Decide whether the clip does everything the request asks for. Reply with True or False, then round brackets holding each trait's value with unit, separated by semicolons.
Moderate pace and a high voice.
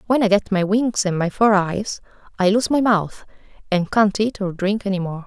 False (230 wpm; 200 Hz)